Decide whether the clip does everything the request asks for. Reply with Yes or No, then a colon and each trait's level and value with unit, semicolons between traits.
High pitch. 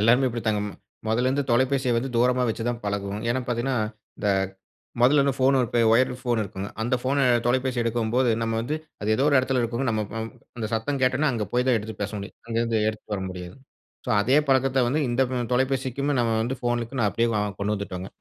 No: low, 120 Hz